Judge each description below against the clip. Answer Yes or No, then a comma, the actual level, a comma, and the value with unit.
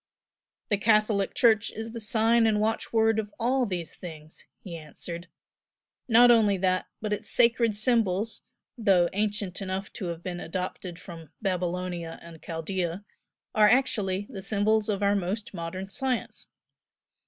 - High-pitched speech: Yes, high, 200 Hz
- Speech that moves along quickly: No, average, 140 wpm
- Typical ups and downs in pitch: Yes, average, 3.5 semitones